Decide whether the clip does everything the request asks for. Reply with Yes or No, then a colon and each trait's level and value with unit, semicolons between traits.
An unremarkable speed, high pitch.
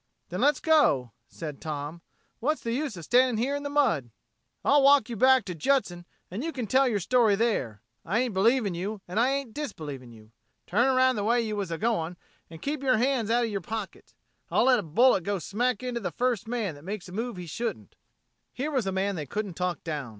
No: fast, 225 wpm; high, 220 Hz